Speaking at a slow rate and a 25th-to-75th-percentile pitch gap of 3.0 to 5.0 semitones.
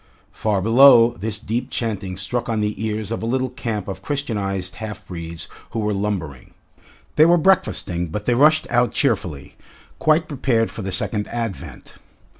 No: average, 165 wpm; average, 3.9 semitones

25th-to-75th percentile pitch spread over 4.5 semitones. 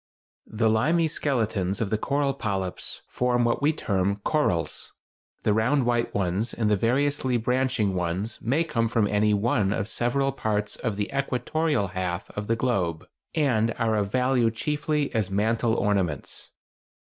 No: average, 4.2 semitones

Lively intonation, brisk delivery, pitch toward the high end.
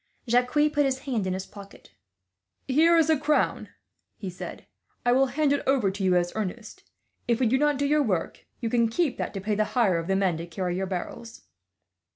Yes: wide, 6.5 semitones; fast, 215 wpm; high, 235 Hz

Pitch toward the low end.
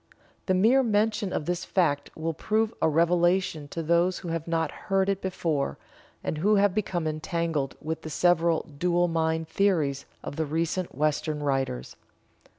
No: medium, 165 Hz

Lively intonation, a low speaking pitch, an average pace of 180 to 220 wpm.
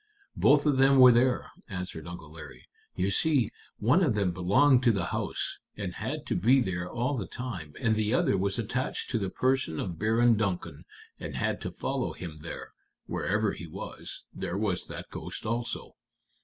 Yes: wide, 5.8 semitones; low, 110 Hz; average, 185 wpm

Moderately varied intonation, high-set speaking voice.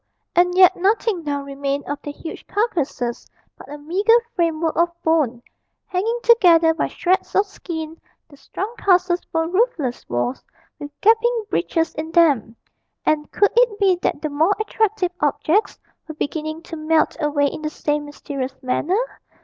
Yes: average, 4.5 semitones; very high, 325 Hz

